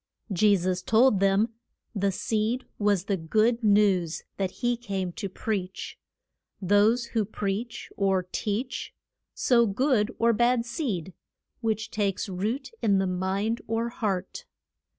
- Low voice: No, high, 210 Hz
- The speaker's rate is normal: No, slow, 130 wpm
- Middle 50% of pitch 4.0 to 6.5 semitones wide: No, average, 3.2 semitones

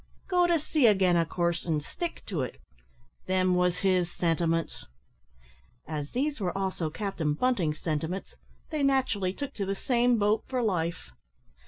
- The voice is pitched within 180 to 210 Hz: Yes, medium, 185 Hz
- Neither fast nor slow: Yes, average, 155 wpm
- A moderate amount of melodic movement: No, wide, 6.5 semitones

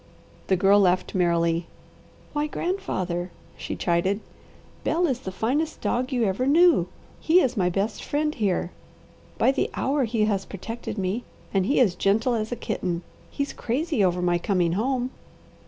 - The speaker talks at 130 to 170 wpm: Yes, average, 160 wpm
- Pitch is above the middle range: Yes, high, 215 Hz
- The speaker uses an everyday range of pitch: No, wide, 6.4 semitones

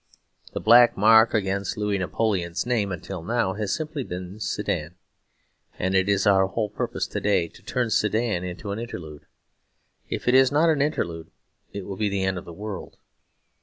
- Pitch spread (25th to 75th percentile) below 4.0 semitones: Yes, average, 3.5 semitones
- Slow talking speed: No, average, 180 wpm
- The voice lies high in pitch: No, low, 100 Hz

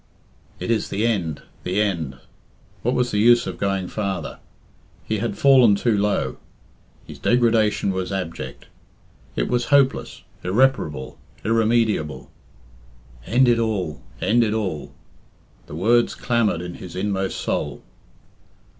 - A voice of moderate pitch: No, low, 105 Hz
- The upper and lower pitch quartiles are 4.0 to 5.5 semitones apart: Yes, average, 4.3 semitones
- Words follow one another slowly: Yes, slow, 130 wpm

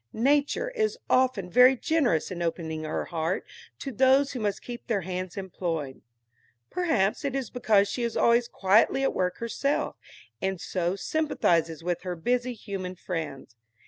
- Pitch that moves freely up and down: Yes, wide, 6.5 semitones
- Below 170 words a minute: Yes, average, 155 wpm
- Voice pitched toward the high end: Yes, high, 200 Hz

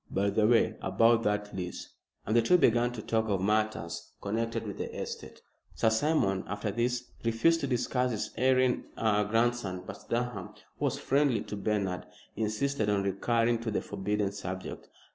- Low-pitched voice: Yes, low, 110 Hz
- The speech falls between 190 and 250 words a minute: No, average, 165 wpm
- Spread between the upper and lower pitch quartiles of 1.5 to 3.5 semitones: Yes, average, 2.9 semitones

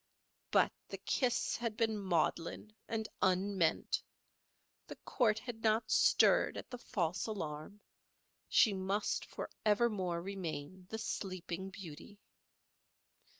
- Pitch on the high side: Yes, high, 200 Hz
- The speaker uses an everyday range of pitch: Yes, average, 3.4 semitones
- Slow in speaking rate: Yes, slow, 105 wpm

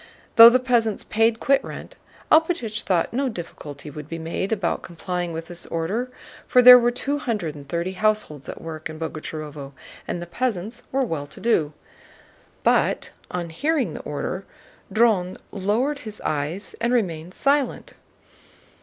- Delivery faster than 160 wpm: No, average, 155 wpm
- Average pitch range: No, wide, 6.6 semitones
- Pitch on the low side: No, high, 190 Hz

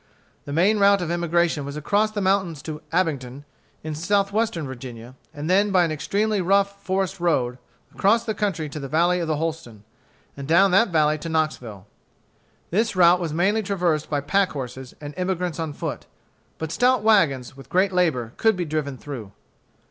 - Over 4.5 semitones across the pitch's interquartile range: Yes, average, 5.0 semitones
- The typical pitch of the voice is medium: Yes, medium, 170 Hz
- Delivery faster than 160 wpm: Yes, average, 180 wpm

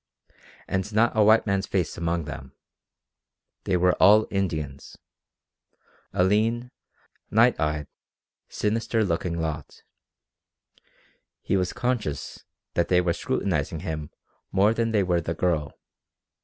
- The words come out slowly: Yes, slow, 120 wpm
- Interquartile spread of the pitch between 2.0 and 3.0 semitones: No, average, 4.6 semitones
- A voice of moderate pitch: No, very low, 90 Hz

